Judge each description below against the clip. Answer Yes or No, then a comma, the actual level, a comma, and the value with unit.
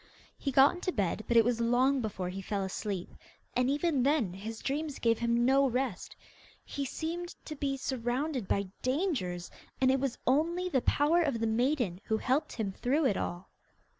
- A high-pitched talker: Yes, very high, 255 Hz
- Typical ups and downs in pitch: Yes, average, 4.6 semitones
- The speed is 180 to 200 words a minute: Yes, average, 185 wpm